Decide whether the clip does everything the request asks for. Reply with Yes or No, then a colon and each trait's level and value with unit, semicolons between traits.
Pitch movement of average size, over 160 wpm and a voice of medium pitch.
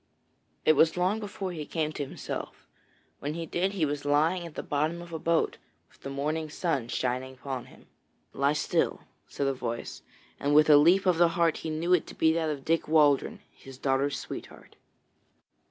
Yes: average, 3.1 semitones; average, 195 wpm; medium, 155 Hz